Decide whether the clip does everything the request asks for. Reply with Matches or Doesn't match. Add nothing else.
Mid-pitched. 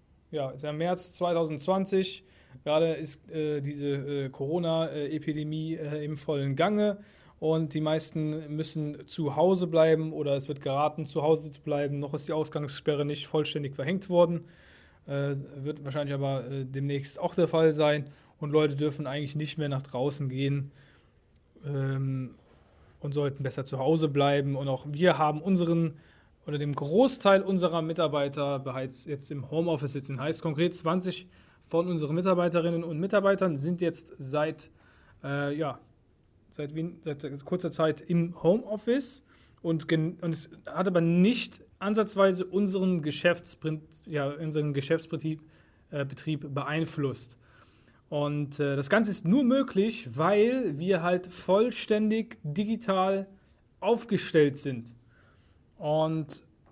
Matches